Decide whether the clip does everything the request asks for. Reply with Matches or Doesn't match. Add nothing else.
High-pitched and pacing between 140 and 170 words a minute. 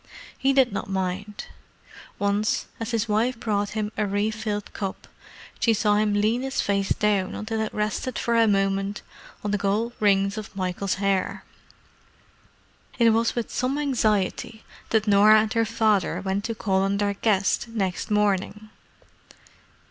Matches